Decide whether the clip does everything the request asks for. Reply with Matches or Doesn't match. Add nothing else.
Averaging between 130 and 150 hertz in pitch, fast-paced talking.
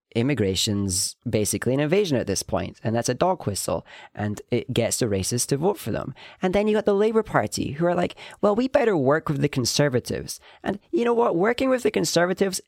Matches